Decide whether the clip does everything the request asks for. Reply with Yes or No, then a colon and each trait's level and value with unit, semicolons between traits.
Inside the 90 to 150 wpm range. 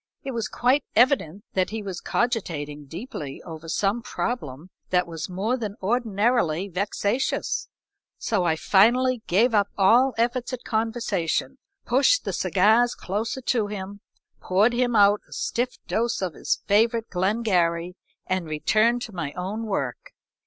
Yes: average, 145 wpm